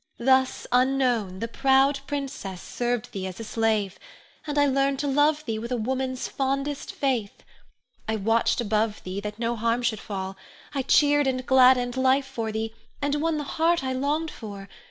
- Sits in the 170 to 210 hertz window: No, very high, 255 Hz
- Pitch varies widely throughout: No, average, 3.8 semitones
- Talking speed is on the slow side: No, average, 175 wpm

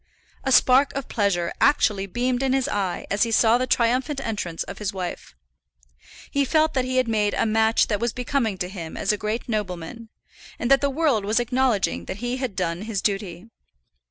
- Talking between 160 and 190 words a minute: No, average, 200 wpm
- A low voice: No, high, 225 Hz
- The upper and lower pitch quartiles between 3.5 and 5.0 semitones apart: Yes, average, 4.4 semitones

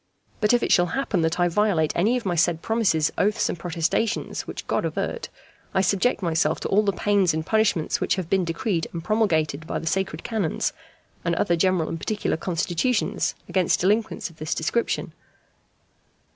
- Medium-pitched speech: Yes, medium, 180 Hz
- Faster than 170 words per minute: Yes, average, 180 wpm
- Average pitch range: Yes, average, 4.3 semitones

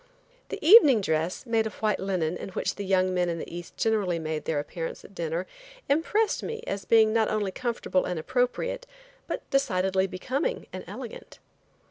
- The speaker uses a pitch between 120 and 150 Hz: No, high, 195 Hz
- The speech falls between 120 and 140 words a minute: No, average, 175 wpm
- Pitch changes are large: Yes, wide, 5.9 semitones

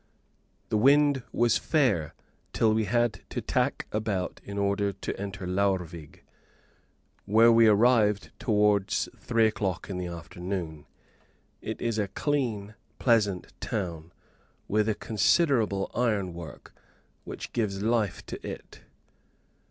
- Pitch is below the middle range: Yes, low, 105 Hz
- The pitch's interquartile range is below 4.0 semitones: Yes, average, 3.2 semitones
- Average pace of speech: No, slow, 120 wpm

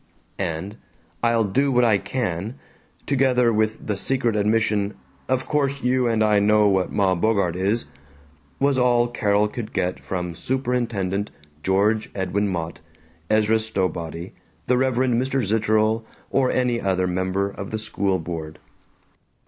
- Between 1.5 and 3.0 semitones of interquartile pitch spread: No, average, 4.1 semitones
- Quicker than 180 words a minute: No, average, 140 wpm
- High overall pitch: No, low, 110 Hz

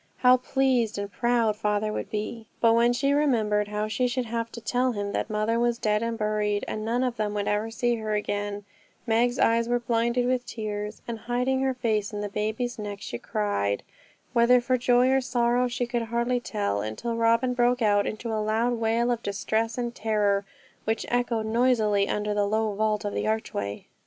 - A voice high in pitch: Yes, high, 225 Hz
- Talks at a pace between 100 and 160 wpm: No, average, 200 wpm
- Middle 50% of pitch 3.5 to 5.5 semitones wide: No, narrow, 2.4 semitones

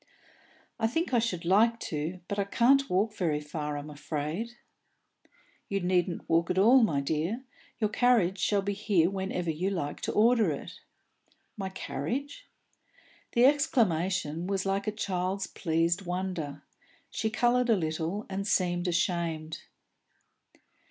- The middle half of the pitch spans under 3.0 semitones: No, average, 4.7 semitones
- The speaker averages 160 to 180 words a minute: No, average, 140 wpm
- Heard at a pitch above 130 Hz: Yes, high, 190 Hz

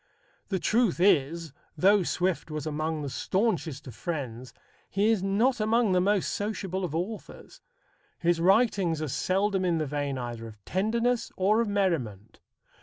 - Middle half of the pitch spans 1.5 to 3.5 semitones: No, average, 5.3 semitones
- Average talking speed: Yes, average, 155 wpm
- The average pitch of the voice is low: No, medium, 180 Hz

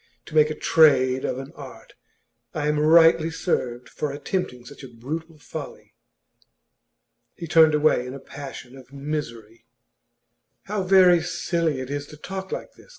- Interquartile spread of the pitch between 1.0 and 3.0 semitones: No, average, 3.7 semitones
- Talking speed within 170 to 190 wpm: No, average, 155 wpm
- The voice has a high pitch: No, medium, 150 Hz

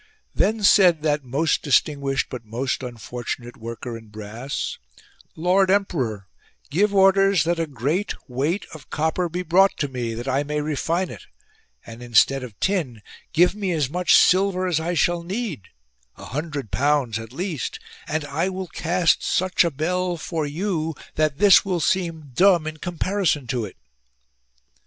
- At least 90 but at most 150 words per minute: No, average, 160 wpm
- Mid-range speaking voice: Yes, medium, 155 Hz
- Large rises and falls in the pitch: Yes, wide, 5.8 semitones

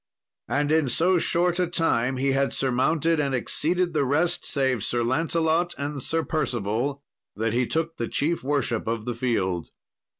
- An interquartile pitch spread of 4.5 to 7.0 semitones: Yes, average, 4.9 semitones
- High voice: No, medium, 140 Hz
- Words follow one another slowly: No, average, 165 wpm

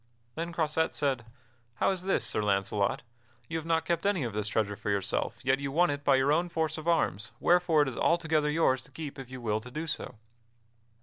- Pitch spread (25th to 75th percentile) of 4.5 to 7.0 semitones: Yes, wide, 5.4 semitones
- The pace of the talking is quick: Yes, fast, 225 wpm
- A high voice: No, medium, 145 Hz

